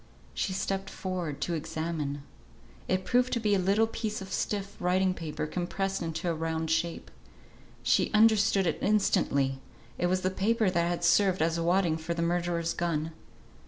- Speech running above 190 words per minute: No, average, 165 wpm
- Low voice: No, medium, 175 Hz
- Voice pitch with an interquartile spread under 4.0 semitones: Yes, average, 3.0 semitones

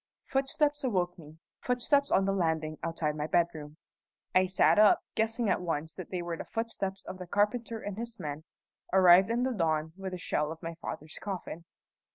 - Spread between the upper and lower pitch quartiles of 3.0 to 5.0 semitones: No, wide, 5.4 semitones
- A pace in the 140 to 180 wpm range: No, average, 190 wpm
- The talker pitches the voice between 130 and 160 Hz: No, medium, 185 Hz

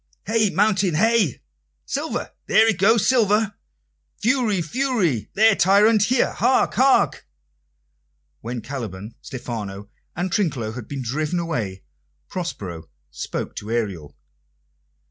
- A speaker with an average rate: No, slow, 110 wpm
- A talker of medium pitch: Yes, medium, 175 Hz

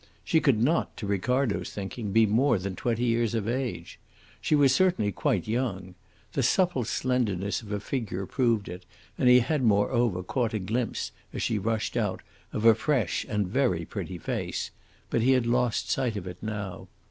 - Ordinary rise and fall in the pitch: Yes, average, 3.8 semitones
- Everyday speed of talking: Yes, average, 180 wpm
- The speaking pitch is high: No, low, 115 Hz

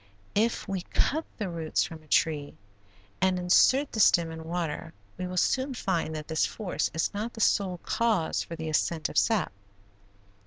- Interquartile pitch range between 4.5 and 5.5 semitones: Yes, average, 4.8 semitones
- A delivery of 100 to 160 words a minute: No, average, 180 wpm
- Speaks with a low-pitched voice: No, medium, 180 Hz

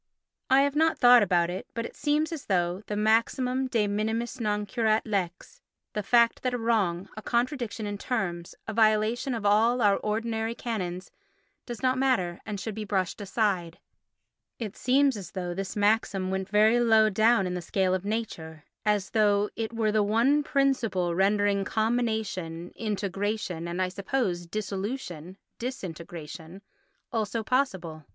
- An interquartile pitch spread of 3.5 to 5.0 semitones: Yes, average, 3.8 semitones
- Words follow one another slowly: No, average, 155 wpm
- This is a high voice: Yes, high, 210 Hz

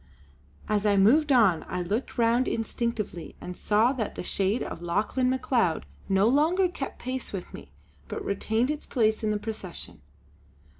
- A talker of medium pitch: No, high, 220 Hz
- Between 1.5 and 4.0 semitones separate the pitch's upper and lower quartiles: No, average, 4.6 semitones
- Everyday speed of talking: Yes, average, 160 wpm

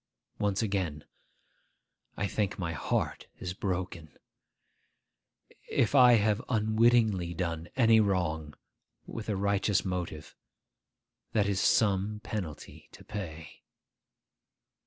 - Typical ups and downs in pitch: Yes, average, 3.7 semitones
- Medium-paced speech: No, slow, 100 wpm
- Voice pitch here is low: Yes, low, 100 Hz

